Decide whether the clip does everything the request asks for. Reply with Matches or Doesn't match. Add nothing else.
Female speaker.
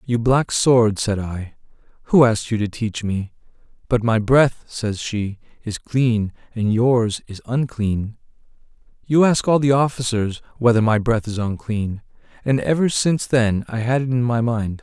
Doesn't match